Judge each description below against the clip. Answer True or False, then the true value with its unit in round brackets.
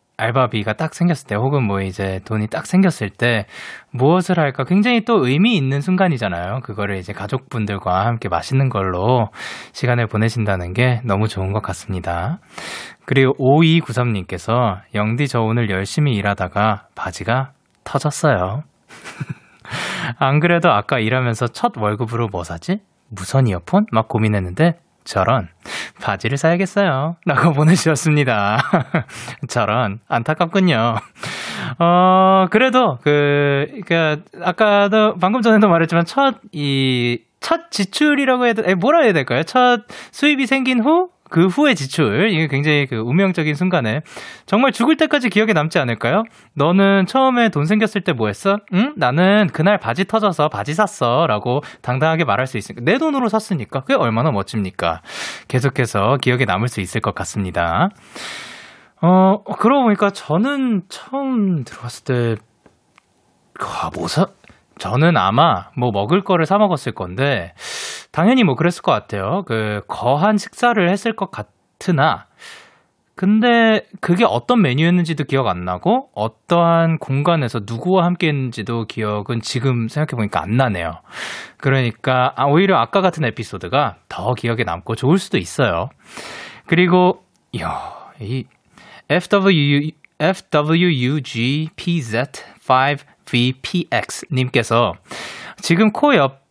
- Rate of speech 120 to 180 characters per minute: False (290 characters per minute)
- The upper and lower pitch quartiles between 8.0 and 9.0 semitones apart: True (8.3 semitones)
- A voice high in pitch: False (145 Hz)